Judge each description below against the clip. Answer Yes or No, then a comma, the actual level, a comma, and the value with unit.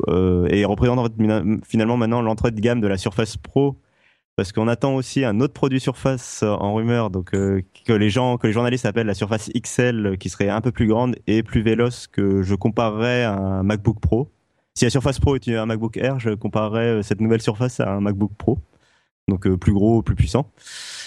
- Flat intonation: No, average, 3.0 semitones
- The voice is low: Yes, low, 110 Hz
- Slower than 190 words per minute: No, average, 215 wpm